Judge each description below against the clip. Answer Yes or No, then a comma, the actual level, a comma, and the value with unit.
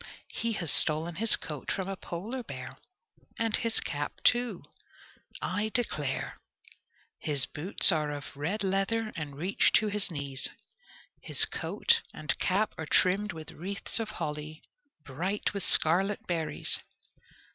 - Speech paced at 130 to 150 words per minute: Yes, slow, 135 wpm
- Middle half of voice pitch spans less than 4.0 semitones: No, wide, 5.5 semitones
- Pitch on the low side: No, medium, 185 Hz